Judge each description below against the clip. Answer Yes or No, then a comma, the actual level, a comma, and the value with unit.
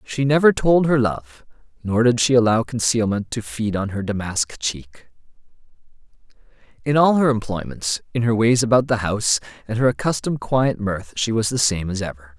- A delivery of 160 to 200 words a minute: Yes, average, 180 wpm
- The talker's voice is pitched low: Yes, low, 115 Hz